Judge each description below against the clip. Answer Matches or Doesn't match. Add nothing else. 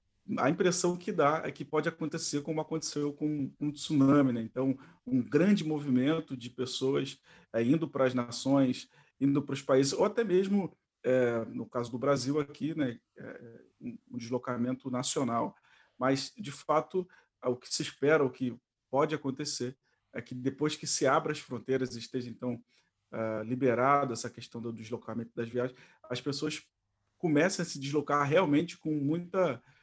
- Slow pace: Doesn't match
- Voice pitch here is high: Doesn't match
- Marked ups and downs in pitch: Doesn't match